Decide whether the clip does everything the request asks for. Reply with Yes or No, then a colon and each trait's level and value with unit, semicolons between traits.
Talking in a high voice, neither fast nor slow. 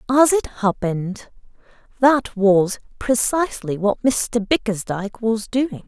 No: high, 225 Hz; slow, 110 wpm